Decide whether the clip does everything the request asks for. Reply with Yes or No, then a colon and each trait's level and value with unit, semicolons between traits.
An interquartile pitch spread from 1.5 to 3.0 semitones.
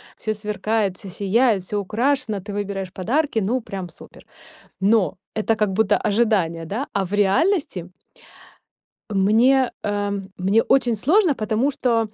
No: average, 3.4 semitones